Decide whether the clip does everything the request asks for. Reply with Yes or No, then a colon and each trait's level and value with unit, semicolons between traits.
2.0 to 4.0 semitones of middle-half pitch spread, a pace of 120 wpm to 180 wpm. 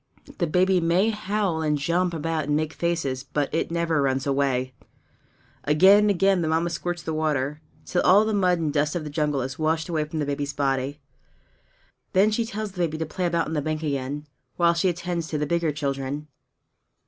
No: average, 3.2 semitones; fast, 205 wpm